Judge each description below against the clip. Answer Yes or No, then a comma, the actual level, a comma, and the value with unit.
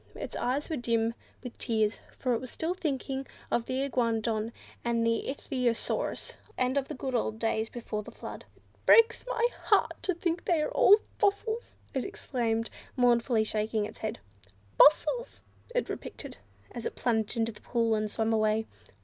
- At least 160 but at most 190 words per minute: Yes, average, 170 wpm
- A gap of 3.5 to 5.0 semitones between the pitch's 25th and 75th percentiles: Yes, average, 3.8 semitones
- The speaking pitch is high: Yes, high, 240 Hz